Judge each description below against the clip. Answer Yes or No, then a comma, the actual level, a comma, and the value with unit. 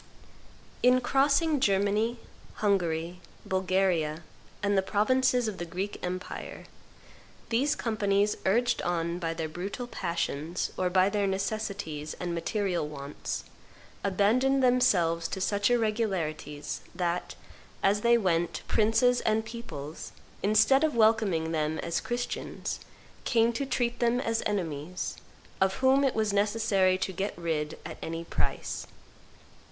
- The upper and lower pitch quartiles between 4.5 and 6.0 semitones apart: Yes, average, 5.1 semitones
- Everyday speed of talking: No, slow, 125 wpm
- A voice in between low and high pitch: No, high, 200 Hz